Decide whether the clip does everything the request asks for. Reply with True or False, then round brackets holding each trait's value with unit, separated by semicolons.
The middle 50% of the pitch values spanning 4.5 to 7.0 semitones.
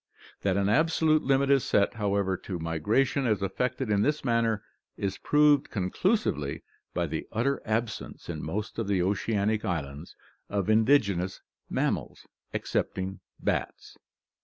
True (5.2 semitones)